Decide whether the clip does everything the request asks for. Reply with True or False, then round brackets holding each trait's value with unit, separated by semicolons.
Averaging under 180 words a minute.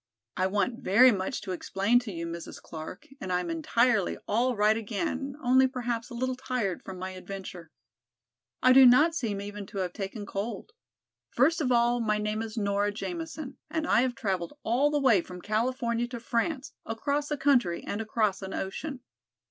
False (185 wpm)